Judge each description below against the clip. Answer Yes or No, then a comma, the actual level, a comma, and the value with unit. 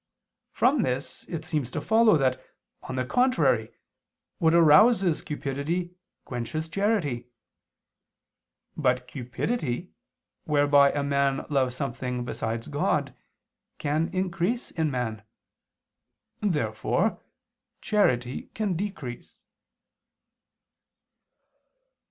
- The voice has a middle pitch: Yes, medium, 145 Hz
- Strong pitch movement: Yes, wide, 6.0 semitones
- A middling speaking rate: No, slow, 85 wpm